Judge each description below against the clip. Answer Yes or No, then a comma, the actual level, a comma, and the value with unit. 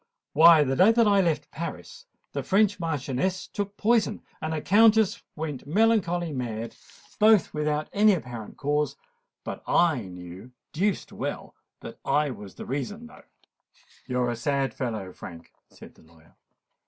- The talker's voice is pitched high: No, medium, 155 Hz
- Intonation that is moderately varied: No, wide, 8.3 semitones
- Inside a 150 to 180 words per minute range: No, average, 140 wpm